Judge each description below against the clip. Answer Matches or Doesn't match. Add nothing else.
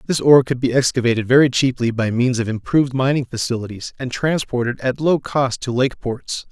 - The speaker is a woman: Doesn't match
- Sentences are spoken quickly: Doesn't match